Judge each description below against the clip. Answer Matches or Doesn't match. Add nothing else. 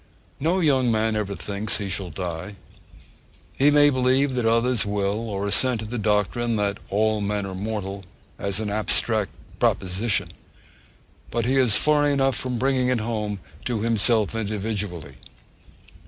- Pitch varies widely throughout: Doesn't match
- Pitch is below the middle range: Matches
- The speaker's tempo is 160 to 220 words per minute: Doesn't match